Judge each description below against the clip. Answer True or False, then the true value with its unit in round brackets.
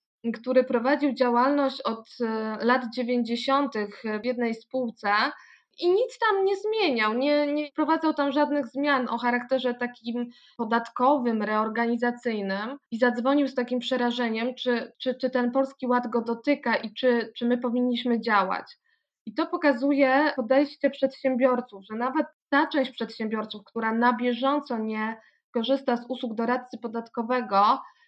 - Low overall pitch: False (250 Hz)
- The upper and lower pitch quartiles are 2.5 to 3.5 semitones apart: True (2.9 semitones)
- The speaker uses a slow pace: False (135 wpm)